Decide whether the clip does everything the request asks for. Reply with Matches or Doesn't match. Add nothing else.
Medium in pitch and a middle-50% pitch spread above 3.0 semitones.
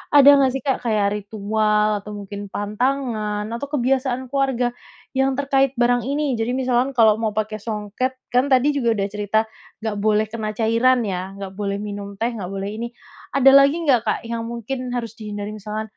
Doesn't match